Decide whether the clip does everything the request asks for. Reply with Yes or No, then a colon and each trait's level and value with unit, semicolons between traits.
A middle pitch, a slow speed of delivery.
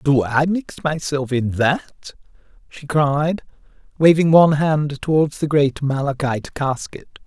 Yes: medium, 145 Hz; slow, 130 wpm